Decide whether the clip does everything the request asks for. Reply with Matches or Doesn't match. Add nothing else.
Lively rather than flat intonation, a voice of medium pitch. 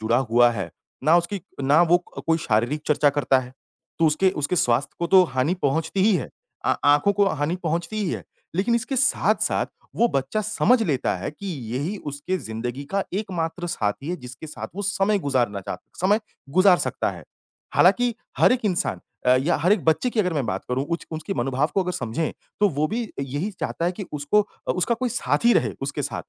Matches